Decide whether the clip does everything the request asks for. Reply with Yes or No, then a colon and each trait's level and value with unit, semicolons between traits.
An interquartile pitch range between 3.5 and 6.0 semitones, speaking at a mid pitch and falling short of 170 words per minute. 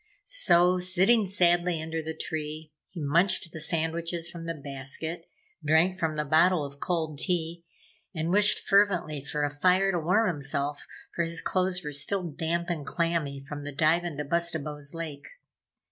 No: average, 2.9 semitones; medium, 165 Hz; average, 160 wpm